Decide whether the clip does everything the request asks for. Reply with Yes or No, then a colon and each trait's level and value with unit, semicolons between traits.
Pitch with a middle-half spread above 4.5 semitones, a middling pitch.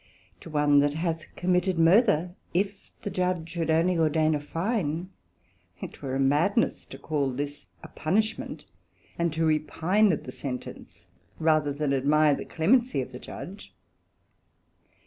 No: average, 3.8 semitones; medium, 160 Hz